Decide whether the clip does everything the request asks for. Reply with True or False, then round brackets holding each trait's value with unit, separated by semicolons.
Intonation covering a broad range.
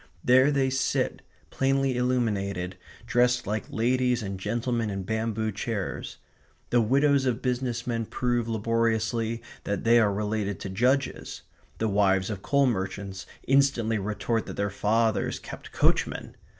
False (3.2 semitones)